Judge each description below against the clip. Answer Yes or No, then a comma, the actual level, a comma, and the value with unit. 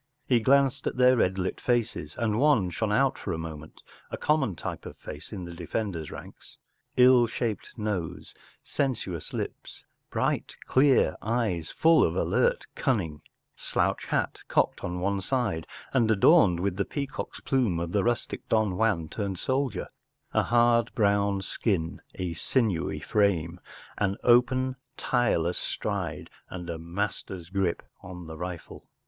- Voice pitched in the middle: No, low, 100 Hz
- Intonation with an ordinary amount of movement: No, wide, 5.7 semitones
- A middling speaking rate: Yes, average, 150 wpm